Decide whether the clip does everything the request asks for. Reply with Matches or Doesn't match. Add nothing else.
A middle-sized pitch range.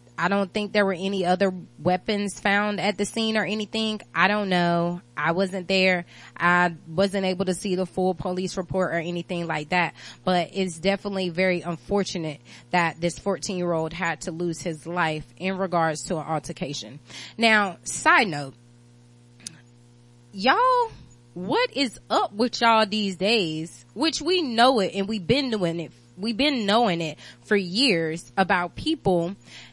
Matches